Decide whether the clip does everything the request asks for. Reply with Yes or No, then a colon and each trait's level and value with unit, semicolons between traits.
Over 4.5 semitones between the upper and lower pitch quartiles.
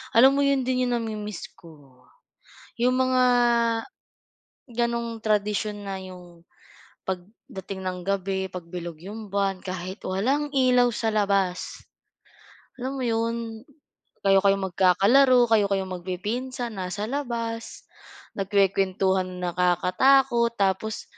No: average, 4.1 semitones